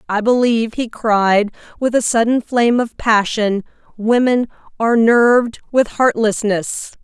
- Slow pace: Yes, slow, 130 wpm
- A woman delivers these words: Yes, female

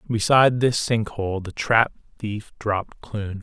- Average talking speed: Yes, average, 155 wpm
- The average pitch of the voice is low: Yes, low, 110 Hz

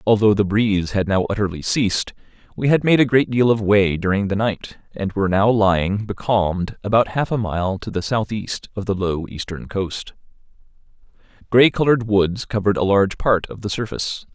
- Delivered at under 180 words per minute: No, average, 190 wpm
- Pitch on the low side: Yes, low, 105 Hz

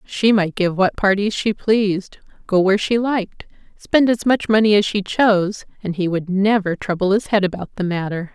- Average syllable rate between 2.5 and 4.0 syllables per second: No, 5.1 syllables/s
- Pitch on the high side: Yes, high, 200 Hz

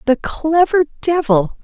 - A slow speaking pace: Yes, slow, 110 wpm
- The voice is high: Yes, very high, 290 Hz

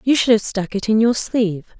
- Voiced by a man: No, female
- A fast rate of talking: Yes, fast, 265 wpm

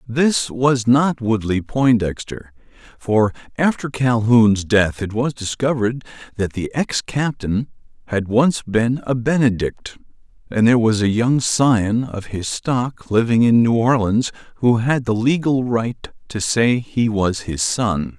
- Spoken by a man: Yes, male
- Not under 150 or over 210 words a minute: No, average, 140 wpm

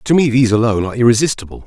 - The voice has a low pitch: Yes, low, 120 Hz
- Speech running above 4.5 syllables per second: Yes, 8.9 syllables/s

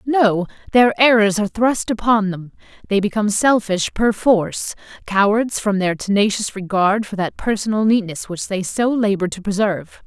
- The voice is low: No, high, 205 Hz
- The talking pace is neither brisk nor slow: Yes, average, 160 wpm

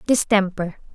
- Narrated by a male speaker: No, female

